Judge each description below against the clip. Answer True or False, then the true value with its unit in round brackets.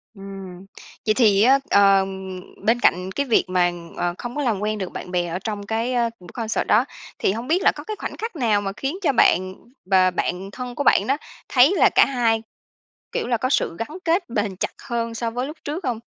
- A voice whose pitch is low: False (225 Hz)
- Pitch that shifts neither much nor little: True (4.8 semitones)